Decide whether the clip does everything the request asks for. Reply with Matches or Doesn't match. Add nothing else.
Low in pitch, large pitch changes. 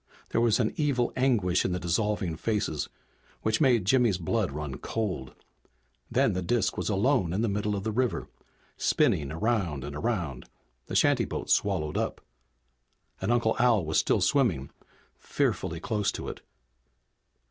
Matches